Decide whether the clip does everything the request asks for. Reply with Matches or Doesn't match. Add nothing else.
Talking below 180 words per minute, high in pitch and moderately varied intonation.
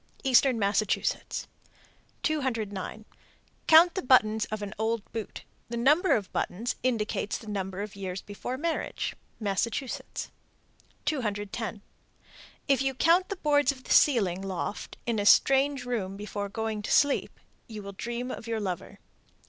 Matches